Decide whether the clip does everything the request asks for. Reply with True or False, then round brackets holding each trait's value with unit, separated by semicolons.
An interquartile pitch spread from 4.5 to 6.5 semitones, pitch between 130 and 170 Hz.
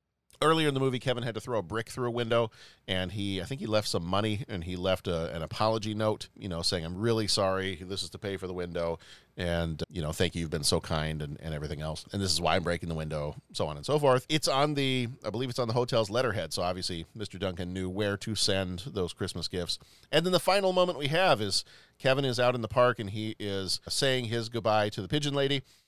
False (5.2 semitones; 105 Hz)